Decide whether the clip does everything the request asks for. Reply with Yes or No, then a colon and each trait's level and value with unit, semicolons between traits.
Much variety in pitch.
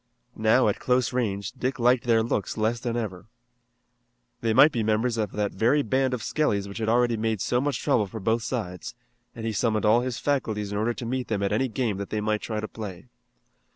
No: average, 2.7 semitones